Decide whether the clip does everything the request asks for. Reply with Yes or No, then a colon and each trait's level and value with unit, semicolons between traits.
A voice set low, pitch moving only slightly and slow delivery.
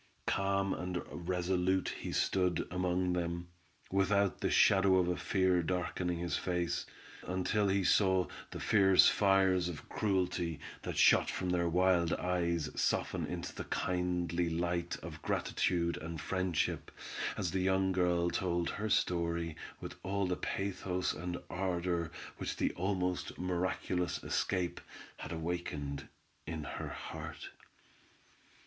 Yes: very low, 90 Hz; narrow, 1.5 semitones; slow, 130 wpm